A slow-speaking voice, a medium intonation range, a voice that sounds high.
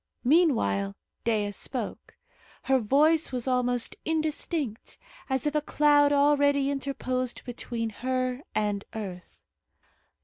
Yes: slow, 105 wpm; average, 4.1 semitones; very high, 255 Hz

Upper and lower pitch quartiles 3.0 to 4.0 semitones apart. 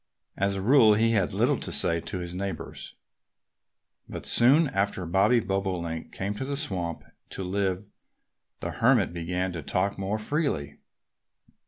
Yes: average, 3.4 semitones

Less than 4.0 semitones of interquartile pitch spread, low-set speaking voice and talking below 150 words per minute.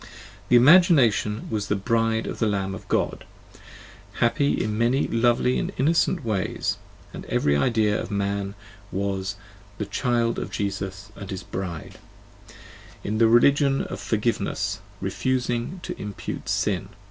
Yes: average, 3.3 semitones; low, 110 Hz; average, 140 wpm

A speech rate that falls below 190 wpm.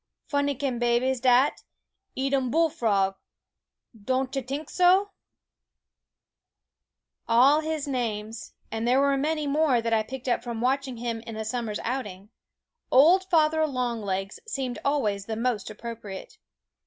Yes: average, 140 wpm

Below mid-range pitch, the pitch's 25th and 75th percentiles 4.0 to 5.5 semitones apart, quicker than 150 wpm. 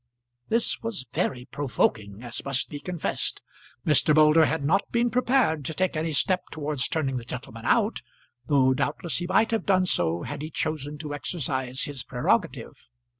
No: medium, 150 Hz; average, 5.1 semitones; average, 170 wpm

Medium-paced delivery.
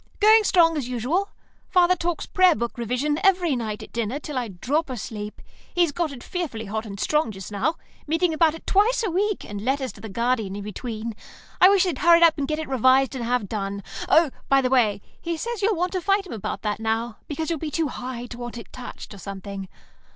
No: fast, 225 wpm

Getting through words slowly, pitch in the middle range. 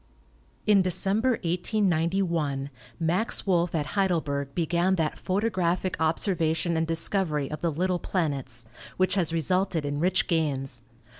Yes: slow, 125 wpm; medium, 170 Hz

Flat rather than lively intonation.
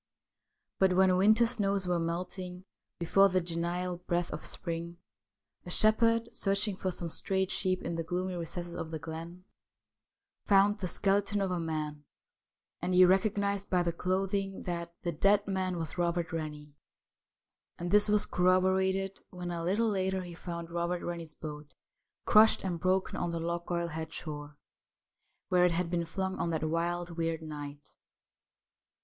Yes: narrow, 2.2 semitones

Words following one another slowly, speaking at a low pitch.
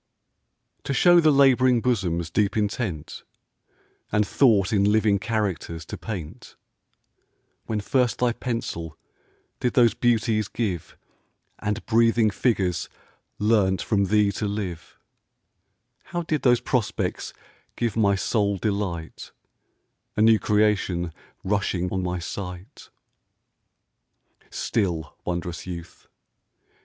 Yes: slow, 105 wpm; low, 105 Hz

